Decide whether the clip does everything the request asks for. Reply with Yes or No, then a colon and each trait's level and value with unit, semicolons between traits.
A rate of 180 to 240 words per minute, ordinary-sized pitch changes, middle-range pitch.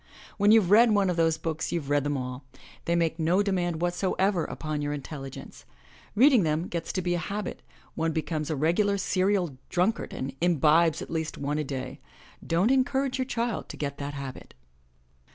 Yes: average, 190 wpm; average, 4.7 semitones; medium, 170 Hz